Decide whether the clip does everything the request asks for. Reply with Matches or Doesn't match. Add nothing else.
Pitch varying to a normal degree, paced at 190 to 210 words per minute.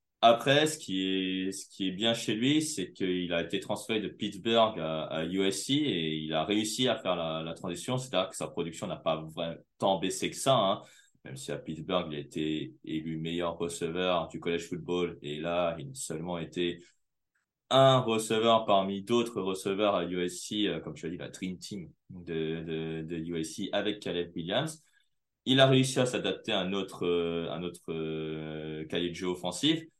Matches